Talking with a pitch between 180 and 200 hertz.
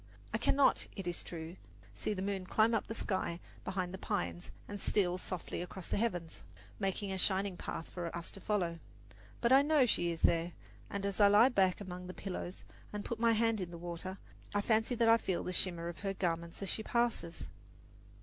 Yes: high, 190 Hz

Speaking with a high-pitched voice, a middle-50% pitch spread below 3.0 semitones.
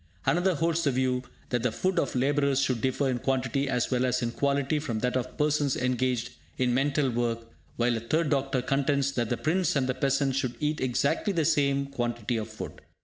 No: low, 135 Hz; narrow, 2.4 semitones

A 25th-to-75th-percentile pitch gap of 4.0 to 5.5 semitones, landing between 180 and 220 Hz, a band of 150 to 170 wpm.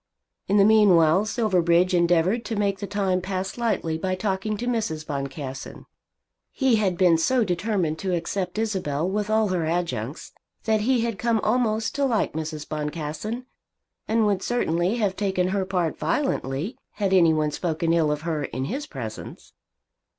Yes: average, 4.9 semitones; medium, 185 Hz; average, 165 wpm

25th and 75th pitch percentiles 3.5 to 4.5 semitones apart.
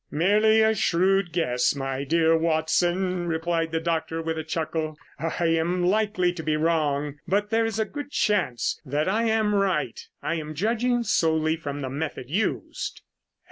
Yes: average, 4.0 semitones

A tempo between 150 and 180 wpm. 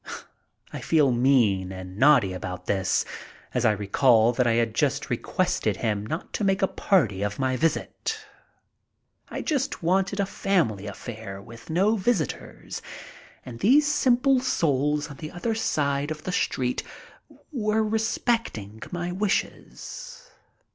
No: slow, 135 wpm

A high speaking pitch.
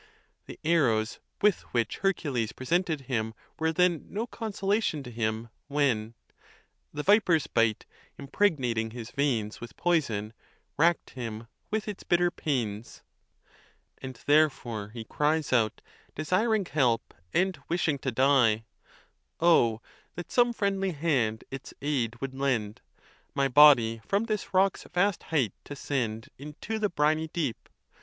No: medium, 140 Hz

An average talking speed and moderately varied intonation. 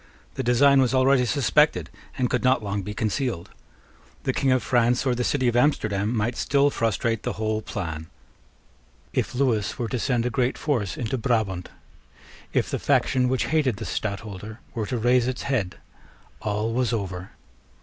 Yes: average, 170 wpm; average, 3.3 semitones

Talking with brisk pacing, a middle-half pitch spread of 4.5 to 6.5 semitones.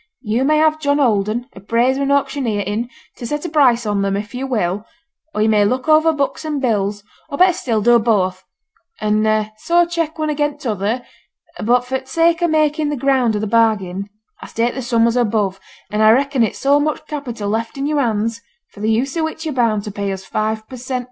Yes: fast, 220 wpm; average, 5.1 semitones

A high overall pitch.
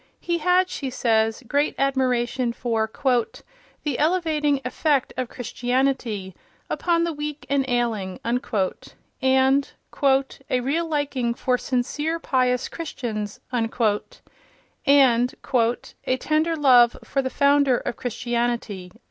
Yes: very high, 260 Hz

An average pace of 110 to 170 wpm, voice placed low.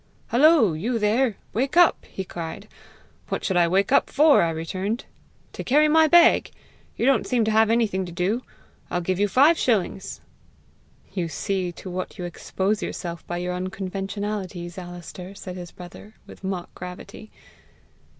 No: average, 160 wpm; high, 195 Hz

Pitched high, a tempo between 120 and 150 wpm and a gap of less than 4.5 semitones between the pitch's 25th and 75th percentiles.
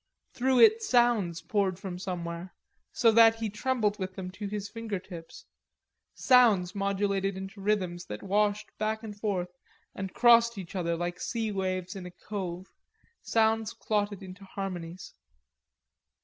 Yes: high, 200 Hz; average, 145 wpm; average, 3.1 semitones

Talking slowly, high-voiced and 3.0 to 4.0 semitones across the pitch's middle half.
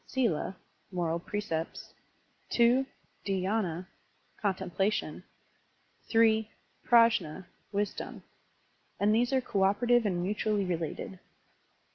Yes: slow, 85 wpm; high, 205 Hz; average, 3.7 semitones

